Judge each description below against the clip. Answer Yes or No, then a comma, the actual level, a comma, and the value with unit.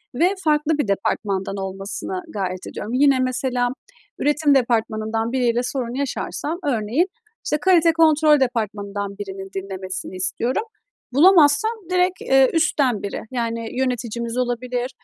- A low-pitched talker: No, high, 245 Hz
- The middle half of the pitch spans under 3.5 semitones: No, wide, 5.6 semitones